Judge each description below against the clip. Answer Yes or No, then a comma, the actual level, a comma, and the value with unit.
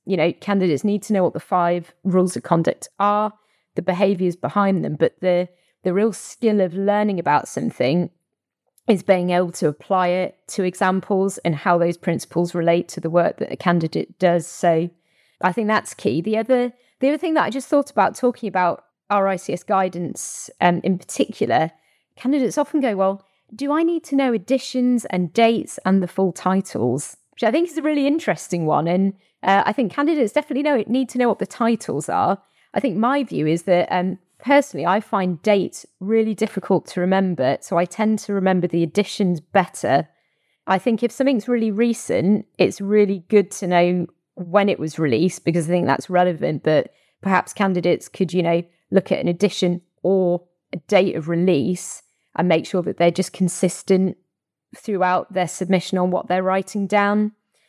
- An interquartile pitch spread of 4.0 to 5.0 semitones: No, average, 3.4 semitones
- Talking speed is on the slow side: No, average, 185 wpm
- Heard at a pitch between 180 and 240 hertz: Yes, high, 190 Hz